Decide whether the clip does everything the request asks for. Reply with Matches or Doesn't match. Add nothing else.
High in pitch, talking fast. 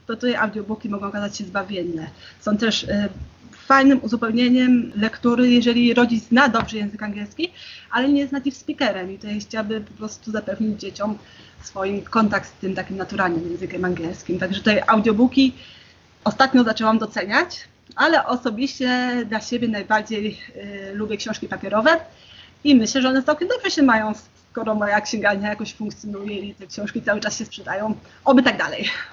Matches